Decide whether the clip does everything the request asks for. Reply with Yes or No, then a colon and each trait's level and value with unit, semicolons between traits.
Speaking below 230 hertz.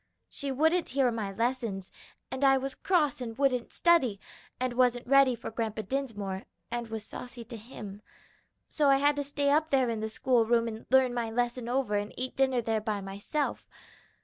No: high, 245 Hz